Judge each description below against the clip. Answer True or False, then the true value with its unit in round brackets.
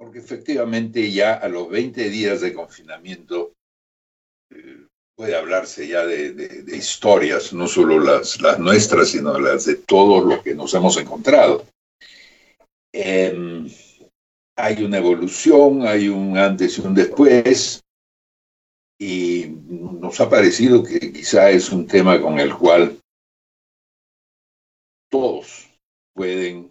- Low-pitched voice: True (105 Hz)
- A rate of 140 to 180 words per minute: False (125 wpm)